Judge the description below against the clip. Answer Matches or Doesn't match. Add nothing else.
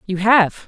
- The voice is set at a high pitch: Matches